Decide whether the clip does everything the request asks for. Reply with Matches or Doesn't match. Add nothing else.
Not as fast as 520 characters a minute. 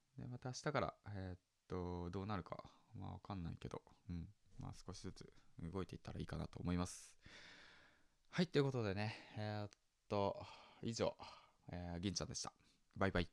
Matches